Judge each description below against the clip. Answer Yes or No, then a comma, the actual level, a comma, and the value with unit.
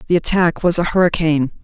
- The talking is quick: No, average, 185 wpm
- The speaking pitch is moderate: Yes, medium, 170 Hz